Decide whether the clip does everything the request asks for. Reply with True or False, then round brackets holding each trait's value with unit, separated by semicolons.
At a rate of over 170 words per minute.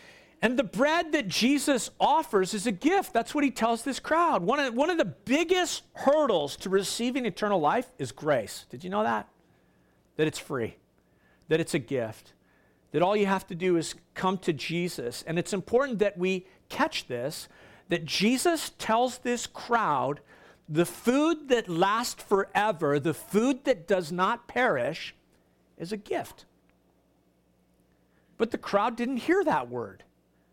False (160 wpm)